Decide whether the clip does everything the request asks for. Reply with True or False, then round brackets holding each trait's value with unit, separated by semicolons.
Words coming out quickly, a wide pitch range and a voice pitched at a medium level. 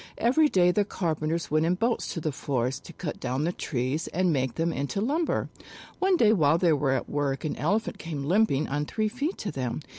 True (215 wpm; 6.5 semitones; 165 Hz)